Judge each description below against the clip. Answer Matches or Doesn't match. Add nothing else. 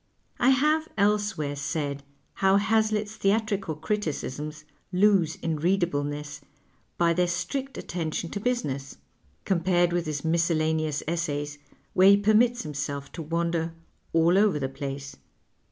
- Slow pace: Matches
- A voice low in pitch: Doesn't match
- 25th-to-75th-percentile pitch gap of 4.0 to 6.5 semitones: Matches